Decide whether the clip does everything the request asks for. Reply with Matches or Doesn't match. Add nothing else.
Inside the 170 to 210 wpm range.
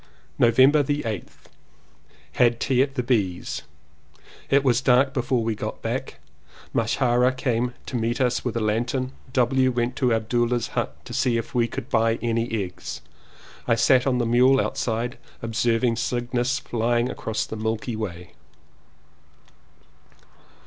Doesn't match